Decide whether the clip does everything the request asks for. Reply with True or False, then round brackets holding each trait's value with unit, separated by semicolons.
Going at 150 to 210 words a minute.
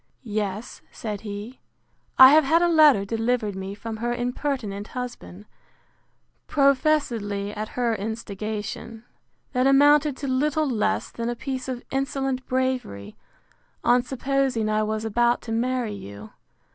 False (135 wpm)